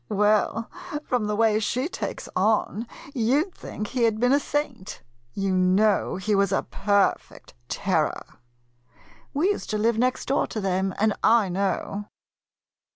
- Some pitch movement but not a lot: Yes, average, 3.4 semitones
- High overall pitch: Yes, high, 215 Hz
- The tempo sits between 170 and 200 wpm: No, average, 155 wpm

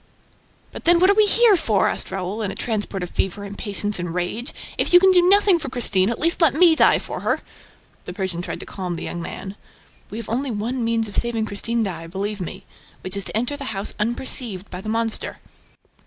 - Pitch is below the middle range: No, high, 220 Hz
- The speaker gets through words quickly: Yes, fast, 225 wpm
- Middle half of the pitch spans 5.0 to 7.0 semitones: Yes, wide, 5.6 semitones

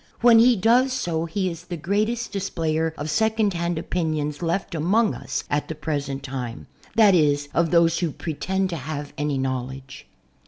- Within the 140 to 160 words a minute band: No, average, 180 wpm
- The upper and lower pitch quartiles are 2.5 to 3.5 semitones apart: No, average, 5.1 semitones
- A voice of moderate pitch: Yes, medium, 165 Hz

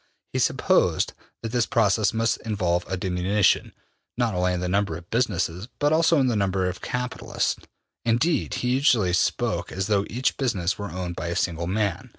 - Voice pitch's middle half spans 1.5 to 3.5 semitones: No, average, 4.8 semitones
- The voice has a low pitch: Yes, low, 100 Hz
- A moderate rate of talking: Yes, average, 180 wpm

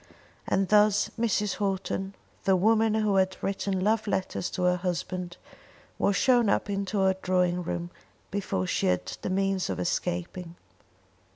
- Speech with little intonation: Yes, narrow, 2.2 semitones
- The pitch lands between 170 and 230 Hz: Yes, high, 190 Hz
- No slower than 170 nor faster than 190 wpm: No, average, 150 wpm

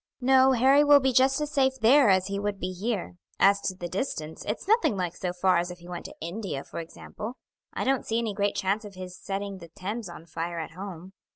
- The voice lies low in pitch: No, high, 200 Hz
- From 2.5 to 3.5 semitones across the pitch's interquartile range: No, average, 5.2 semitones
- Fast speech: Yes, fast, 240 wpm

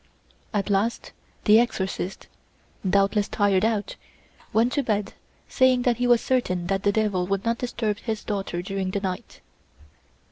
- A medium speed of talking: Yes, average, 150 wpm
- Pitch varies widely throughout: No, average, 2.9 semitones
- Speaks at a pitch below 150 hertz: No, high, 205 Hz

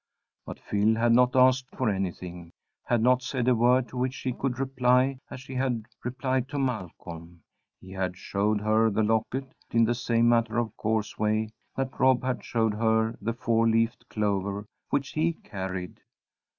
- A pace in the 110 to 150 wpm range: No, average, 175 wpm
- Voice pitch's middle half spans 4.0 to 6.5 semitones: No, average, 3.2 semitones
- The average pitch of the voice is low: Yes, low, 115 Hz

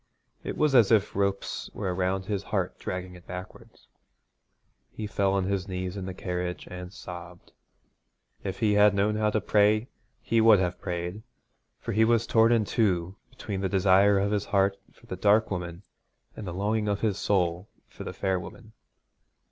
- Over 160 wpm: Yes, average, 180 wpm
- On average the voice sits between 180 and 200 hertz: No, low, 100 Hz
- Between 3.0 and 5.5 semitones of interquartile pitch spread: No, narrow, 2.5 semitones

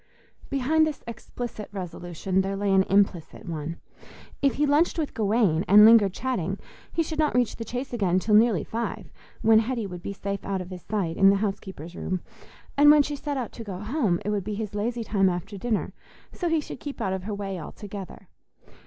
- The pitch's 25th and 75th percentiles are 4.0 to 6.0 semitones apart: Yes, average, 4.3 semitones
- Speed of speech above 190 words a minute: Yes, fast, 205 wpm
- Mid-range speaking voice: No, high, 205 Hz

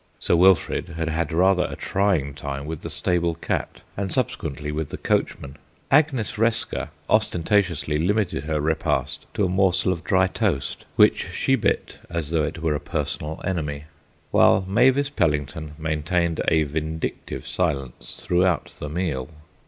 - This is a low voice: Yes, very low, 85 Hz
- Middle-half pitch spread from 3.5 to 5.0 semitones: Yes, average, 3.9 semitones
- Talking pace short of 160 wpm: Yes, average, 150 wpm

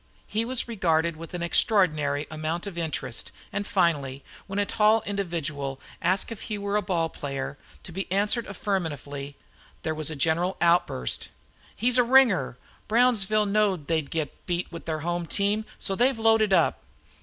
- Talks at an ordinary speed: Yes, average, 170 wpm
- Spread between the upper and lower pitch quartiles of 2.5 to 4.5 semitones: No, average, 4.9 semitones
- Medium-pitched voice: Yes, medium, 180 Hz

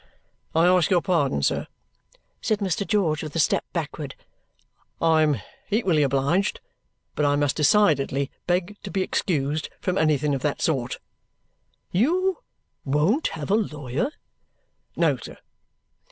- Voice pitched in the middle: Yes, medium, 160 Hz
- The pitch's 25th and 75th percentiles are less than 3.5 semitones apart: No, average, 5.2 semitones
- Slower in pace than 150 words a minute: Yes, slow, 135 wpm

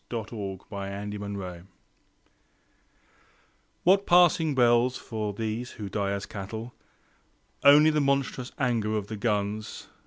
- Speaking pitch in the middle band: No, low, 110 Hz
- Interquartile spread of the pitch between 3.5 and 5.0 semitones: Yes, average, 3.9 semitones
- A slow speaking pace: Yes, slow, 120 wpm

